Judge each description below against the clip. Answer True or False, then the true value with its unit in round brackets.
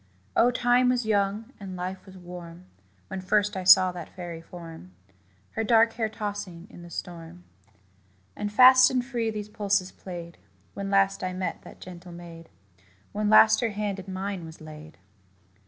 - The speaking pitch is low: False (190 Hz)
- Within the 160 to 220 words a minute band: True (170 wpm)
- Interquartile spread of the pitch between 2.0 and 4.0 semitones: True (3.4 semitones)